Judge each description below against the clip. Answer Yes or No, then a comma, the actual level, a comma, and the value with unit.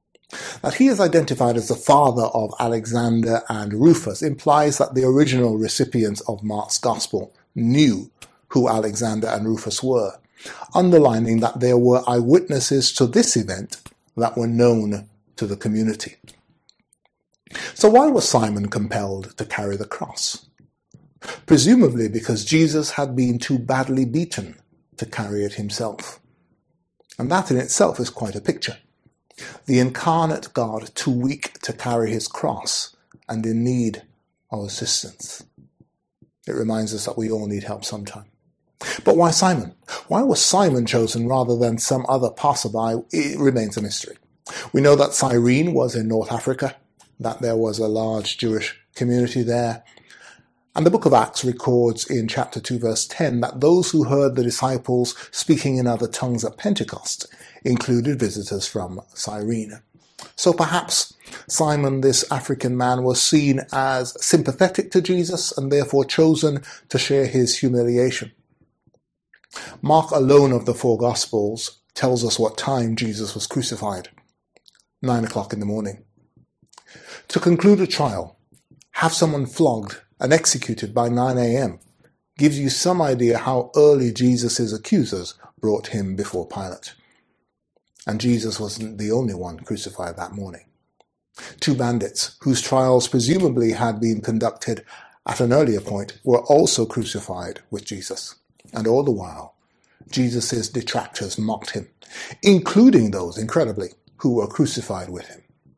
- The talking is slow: No, average, 145 wpm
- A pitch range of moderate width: Yes, average, 3.6 semitones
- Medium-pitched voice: No, low, 120 Hz